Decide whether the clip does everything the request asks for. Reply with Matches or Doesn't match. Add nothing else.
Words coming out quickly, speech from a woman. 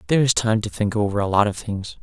Doesn't match